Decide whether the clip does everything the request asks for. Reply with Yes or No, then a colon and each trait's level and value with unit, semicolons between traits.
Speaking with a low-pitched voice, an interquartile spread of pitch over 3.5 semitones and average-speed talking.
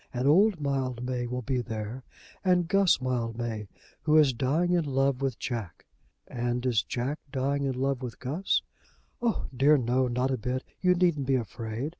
No: low, 130 Hz; average, 3.1 semitones; average, 170 wpm